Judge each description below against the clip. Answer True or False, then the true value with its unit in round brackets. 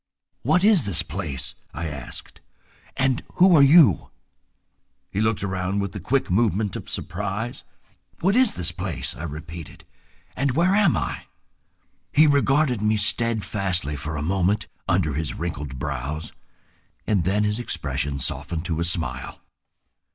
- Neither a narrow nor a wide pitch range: False (7.6 semitones)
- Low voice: True (100 Hz)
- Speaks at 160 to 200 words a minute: False (145 wpm)